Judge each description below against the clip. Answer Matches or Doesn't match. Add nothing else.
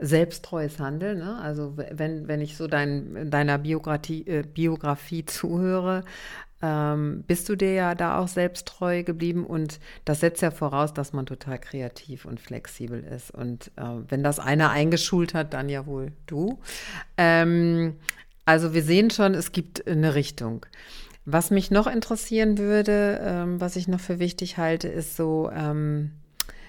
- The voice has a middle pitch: Matches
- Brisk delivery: Doesn't match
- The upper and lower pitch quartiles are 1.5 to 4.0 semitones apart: Matches